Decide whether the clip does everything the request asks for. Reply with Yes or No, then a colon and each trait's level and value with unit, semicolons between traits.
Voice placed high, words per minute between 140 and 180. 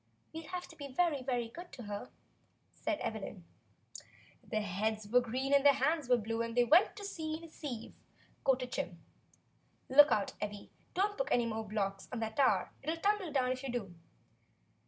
No: very high, 255 Hz; average, 190 wpm